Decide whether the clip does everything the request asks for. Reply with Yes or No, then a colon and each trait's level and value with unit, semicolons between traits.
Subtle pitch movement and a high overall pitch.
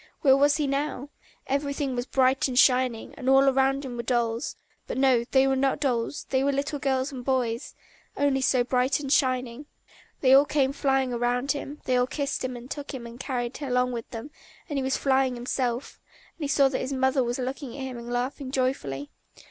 Yes: narrow, 1.8 semitones; very high, 265 Hz